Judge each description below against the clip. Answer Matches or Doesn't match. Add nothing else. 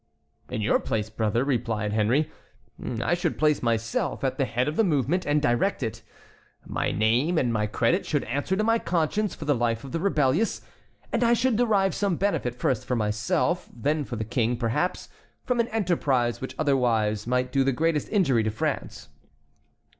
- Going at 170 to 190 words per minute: Matches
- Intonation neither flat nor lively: Doesn't match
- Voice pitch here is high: Doesn't match